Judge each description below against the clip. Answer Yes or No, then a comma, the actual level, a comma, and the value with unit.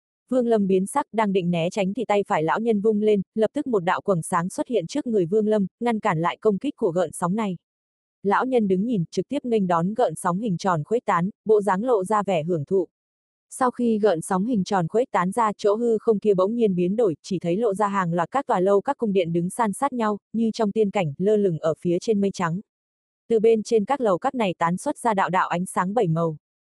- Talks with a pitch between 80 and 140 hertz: No, high, 205 Hz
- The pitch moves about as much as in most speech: Yes, average, 3.8 semitones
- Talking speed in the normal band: No, fast, 265 wpm